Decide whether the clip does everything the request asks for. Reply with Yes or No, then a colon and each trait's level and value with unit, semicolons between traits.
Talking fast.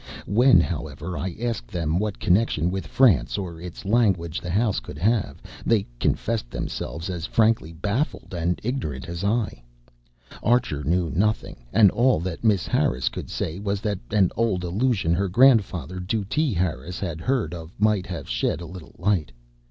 No: average, 165 wpm